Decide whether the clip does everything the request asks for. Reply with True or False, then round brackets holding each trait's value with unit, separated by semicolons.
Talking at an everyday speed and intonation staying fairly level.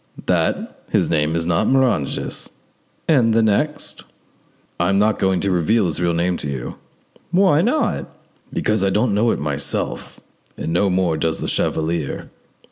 False (160 wpm; 5.4 semitones)